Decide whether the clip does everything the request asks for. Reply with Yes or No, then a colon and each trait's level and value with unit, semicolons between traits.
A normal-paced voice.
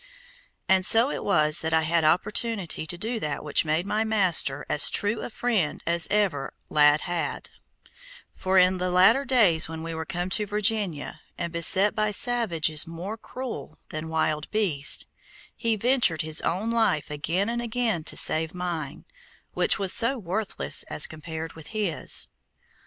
Yes: average, 165 wpm